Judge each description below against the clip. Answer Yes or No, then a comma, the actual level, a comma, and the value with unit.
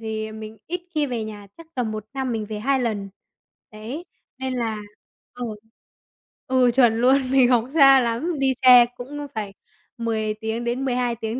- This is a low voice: No, high, 240 Hz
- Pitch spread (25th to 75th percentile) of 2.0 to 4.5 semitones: Yes, average, 3.2 semitones